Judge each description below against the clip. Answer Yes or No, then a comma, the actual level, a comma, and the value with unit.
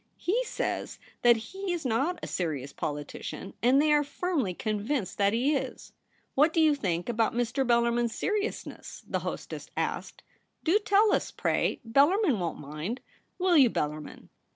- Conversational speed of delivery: Yes, average, 175 wpm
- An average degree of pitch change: No, wide, 7.7 semitones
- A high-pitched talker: Yes, high, 245 Hz